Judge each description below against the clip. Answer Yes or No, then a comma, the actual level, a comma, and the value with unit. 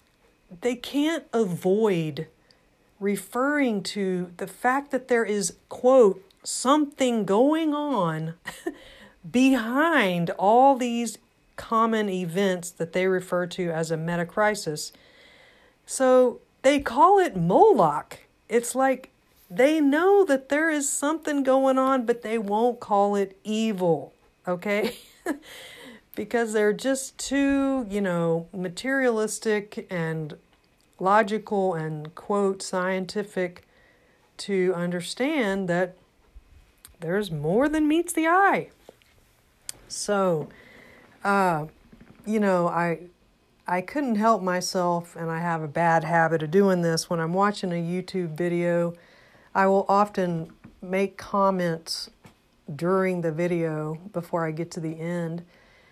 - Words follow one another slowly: Yes, slow, 115 wpm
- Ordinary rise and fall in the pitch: No, wide, 6.3 semitones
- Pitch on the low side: No, high, 195 Hz